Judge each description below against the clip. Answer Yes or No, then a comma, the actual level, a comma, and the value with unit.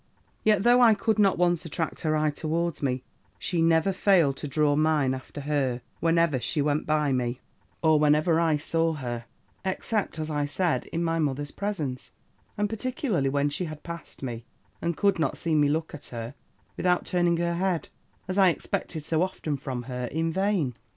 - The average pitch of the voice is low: No, medium, 160 Hz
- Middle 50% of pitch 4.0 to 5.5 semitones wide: No, average, 3.5 semitones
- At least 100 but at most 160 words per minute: No, average, 185 wpm